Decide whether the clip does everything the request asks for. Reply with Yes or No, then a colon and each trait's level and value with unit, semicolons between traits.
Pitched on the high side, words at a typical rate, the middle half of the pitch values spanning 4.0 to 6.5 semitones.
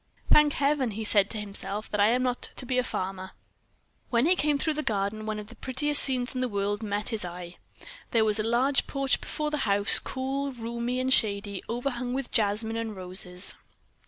No: high, 230 Hz; fast, 210 wpm; average, 4.3 semitones